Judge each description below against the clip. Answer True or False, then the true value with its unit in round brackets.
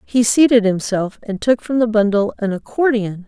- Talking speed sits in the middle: True (165 wpm)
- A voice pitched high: True (220 Hz)